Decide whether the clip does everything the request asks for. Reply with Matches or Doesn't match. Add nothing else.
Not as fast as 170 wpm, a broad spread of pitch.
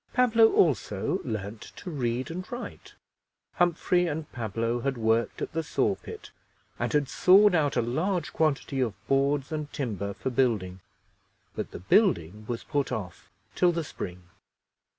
Matches